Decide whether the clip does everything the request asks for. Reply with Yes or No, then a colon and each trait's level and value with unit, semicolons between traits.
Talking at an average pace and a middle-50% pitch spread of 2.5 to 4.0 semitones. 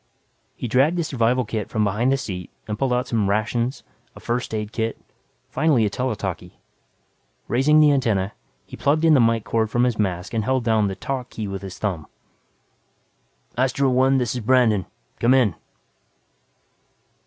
Yes: average, 175 wpm; average, 3.6 semitones